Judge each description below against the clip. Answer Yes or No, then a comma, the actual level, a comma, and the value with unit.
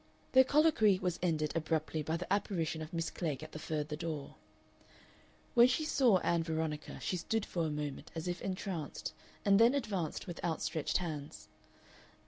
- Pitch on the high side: No, medium, 165 Hz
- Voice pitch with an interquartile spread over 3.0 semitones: Yes, average, 4.1 semitones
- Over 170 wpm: No, average, 165 wpm